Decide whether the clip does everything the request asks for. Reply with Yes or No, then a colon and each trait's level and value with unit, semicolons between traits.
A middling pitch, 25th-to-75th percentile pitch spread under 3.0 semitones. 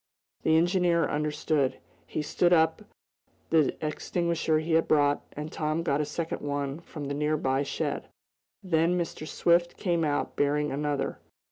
Yes: medium, 155 Hz; narrow, 2.4 semitones